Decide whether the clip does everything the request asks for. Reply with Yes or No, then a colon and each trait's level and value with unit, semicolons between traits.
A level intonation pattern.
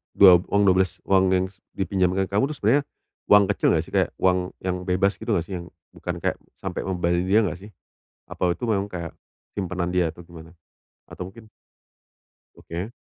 Yes: narrow, 2.0 semitones